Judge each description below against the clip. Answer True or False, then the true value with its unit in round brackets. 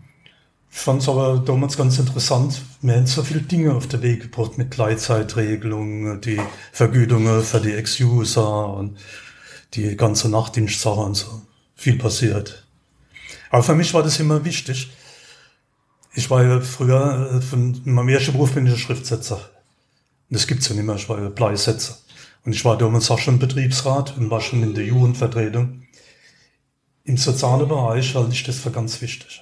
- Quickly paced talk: False (165 wpm)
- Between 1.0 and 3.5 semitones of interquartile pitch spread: True (3.0 semitones)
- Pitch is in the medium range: False (125 Hz)